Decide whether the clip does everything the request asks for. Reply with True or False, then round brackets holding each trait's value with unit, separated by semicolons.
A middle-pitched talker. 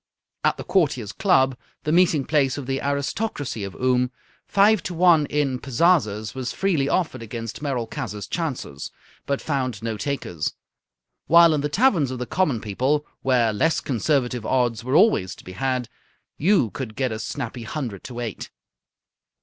False (130 Hz)